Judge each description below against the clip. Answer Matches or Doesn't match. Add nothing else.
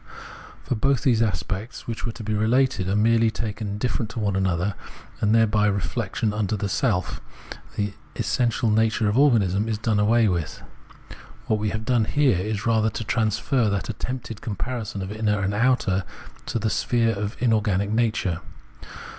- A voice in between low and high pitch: Doesn't match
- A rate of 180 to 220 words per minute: Doesn't match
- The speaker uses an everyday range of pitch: Doesn't match